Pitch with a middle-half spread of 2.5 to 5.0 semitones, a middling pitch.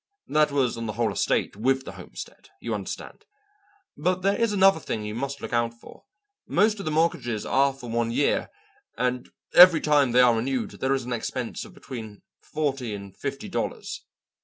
No: average, 4.5 semitones; low, 130 Hz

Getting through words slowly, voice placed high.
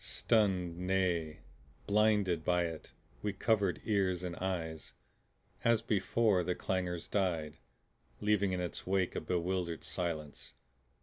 No: slow, 120 wpm; very low, 90 Hz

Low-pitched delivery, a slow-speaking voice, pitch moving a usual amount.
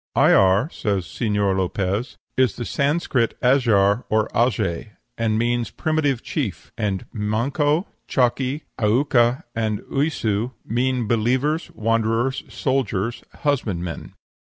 Yes: low, 115 Hz; slow, 105 wpm; average, 4.0 semitones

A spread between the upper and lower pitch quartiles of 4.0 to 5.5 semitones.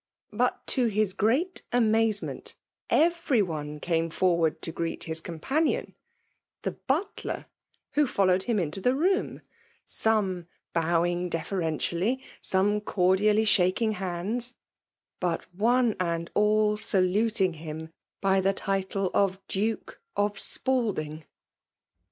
Yes: average, 4.6 semitones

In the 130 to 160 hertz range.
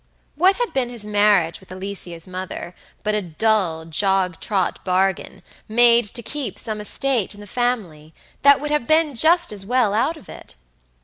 No: high, 210 Hz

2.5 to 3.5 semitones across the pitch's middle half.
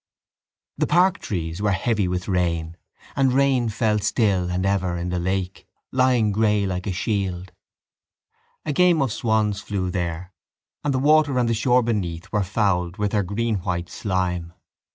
No: average, 4.5 semitones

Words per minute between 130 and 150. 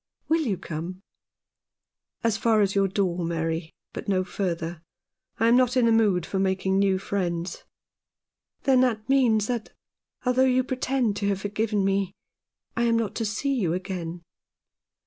No: average, 165 wpm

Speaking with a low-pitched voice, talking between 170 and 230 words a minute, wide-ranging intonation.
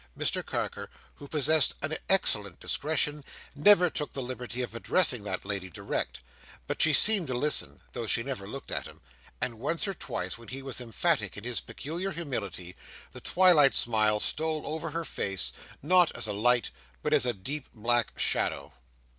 Yes: low, 130 Hz; average, 175 wpm; wide, 5.8 semitones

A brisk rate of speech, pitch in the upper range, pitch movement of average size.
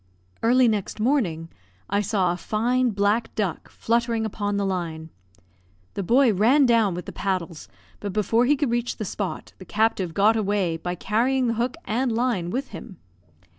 No: average, 170 wpm; high, 215 Hz; average, 4.0 semitones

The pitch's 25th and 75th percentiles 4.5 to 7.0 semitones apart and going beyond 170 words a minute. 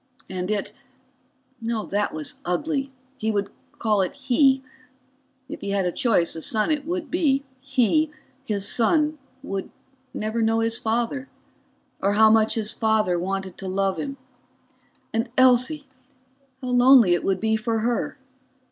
No: average, 5.0 semitones; average, 145 wpm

